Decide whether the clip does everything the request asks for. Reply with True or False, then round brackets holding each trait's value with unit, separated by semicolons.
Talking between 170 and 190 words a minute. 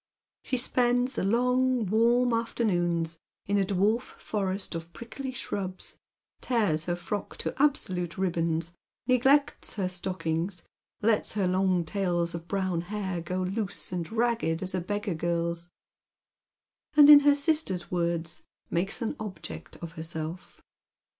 False (135 wpm)